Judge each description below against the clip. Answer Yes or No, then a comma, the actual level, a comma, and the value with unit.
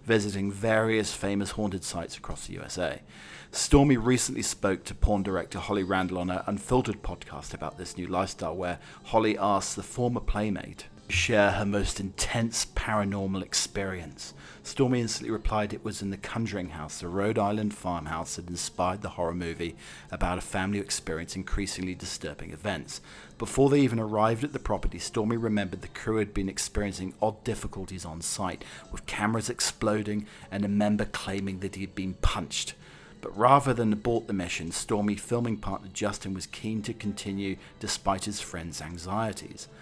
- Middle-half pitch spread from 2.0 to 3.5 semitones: Yes, average, 2.9 semitones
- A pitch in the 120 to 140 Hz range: No, low, 100 Hz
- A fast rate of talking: No, average, 165 wpm